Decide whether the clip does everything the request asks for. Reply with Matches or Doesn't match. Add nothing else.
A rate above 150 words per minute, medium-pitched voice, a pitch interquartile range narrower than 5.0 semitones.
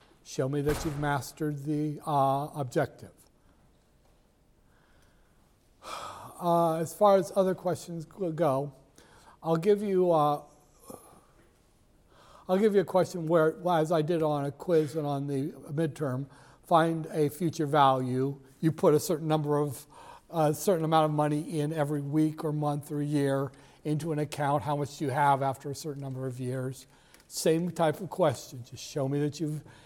Matches